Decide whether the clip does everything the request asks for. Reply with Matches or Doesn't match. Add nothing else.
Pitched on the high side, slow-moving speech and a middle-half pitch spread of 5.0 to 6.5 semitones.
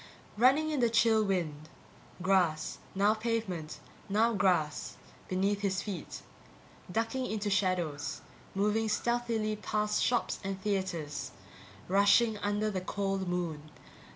Doesn't match